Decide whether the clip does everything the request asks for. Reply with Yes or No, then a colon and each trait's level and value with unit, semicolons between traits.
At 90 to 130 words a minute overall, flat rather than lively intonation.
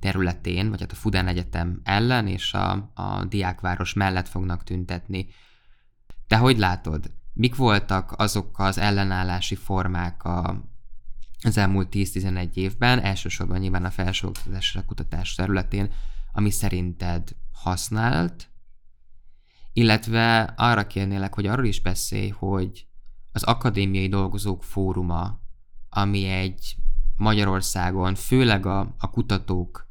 Yes: average, 110 wpm; narrow, 2.2 semitones